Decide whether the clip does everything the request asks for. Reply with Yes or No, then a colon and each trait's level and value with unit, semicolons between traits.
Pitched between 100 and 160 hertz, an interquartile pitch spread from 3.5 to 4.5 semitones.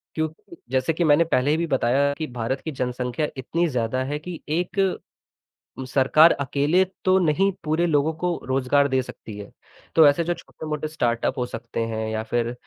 Yes: medium, 140 Hz; average, 4.1 semitones